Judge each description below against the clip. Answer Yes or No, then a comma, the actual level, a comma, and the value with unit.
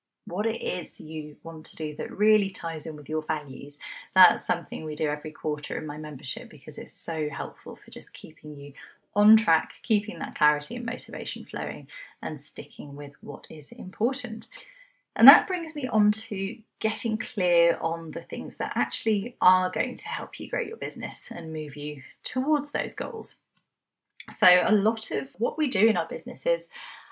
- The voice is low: No, medium, 185 Hz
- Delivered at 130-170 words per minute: No, average, 180 wpm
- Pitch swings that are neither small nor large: No, wide, 6.6 semitones